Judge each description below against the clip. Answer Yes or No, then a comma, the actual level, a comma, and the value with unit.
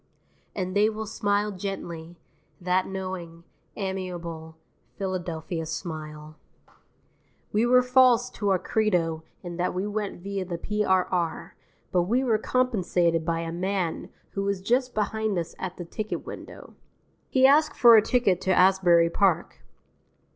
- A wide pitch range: No, average, 3.7 semitones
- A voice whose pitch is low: No, high, 190 Hz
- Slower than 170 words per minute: Yes, average, 140 wpm